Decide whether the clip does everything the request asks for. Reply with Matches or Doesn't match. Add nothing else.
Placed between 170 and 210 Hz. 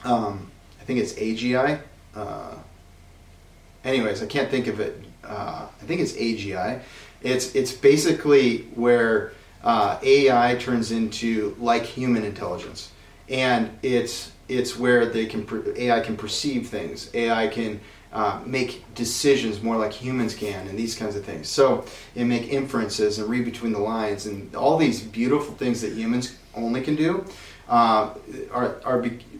Doesn't match